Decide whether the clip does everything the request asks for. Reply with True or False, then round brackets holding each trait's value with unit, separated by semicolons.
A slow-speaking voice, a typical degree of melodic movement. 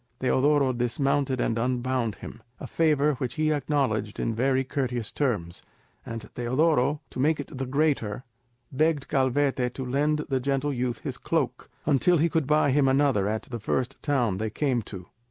False (170 wpm; 3.2 semitones)